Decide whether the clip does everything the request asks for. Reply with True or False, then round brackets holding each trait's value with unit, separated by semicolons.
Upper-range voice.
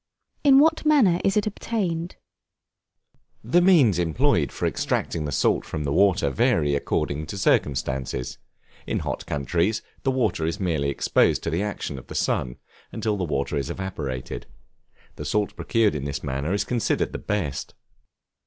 False (85 Hz)